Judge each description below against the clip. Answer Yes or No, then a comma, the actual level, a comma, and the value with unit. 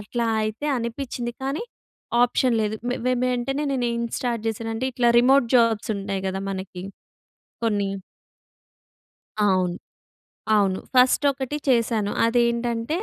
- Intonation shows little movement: No, average, 3.2 semitones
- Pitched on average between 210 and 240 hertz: Yes, high, 235 Hz